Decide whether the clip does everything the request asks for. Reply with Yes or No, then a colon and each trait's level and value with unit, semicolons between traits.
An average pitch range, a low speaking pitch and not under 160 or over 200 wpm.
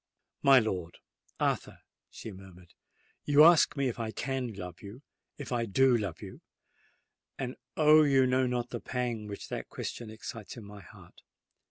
No: average, 4.5 semitones; low, 120 Hz; average, 145 wpm